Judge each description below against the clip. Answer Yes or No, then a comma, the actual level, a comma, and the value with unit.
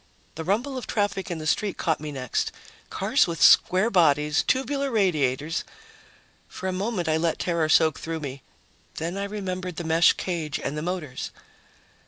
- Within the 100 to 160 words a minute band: No, average, 170 wpm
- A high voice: No, medium, 170 Hz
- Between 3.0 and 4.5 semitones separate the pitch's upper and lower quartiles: Yes, average, 3.9 semitones